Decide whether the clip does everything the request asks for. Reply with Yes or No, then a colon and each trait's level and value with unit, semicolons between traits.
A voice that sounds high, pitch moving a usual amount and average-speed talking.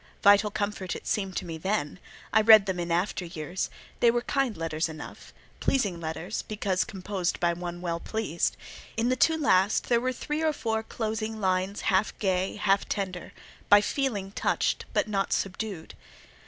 Yes: high, 200 Hz; average, 3.6 semitones; average, 170 wpm